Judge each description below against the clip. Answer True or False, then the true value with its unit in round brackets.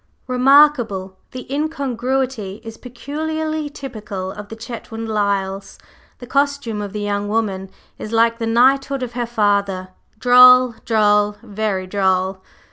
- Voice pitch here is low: False (225 Hz)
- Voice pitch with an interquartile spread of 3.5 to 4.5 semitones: True (4.0 semitones)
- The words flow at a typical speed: False (130 wpm)